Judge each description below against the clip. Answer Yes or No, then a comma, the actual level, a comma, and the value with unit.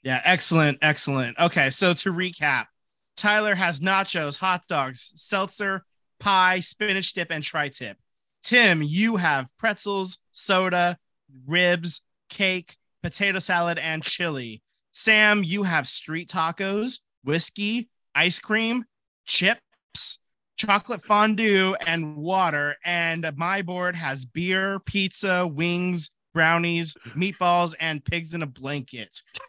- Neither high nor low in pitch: Yes, medium, 175 Hz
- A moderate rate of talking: No, slow, 115 wpm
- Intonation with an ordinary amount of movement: Yes, average, 3.7 semitones